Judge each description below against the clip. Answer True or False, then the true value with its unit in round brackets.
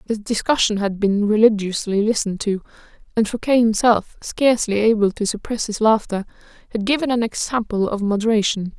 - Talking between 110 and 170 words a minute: True (150 wpm)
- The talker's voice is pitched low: False (215 Hz)